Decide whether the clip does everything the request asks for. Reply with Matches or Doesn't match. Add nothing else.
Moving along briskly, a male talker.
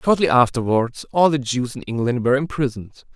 Doesn't match